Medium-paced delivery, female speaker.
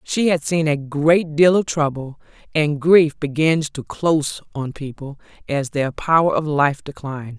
Yes: average, 170 wpm; female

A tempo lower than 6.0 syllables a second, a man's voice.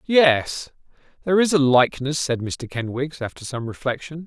Yes: 5.0 syllables/s; male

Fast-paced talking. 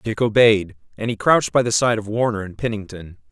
Yes: fast, 215 wpm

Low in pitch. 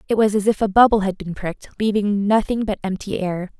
No: high, 205 Hz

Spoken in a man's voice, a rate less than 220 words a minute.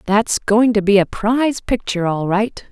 No: female; average, 200 wpm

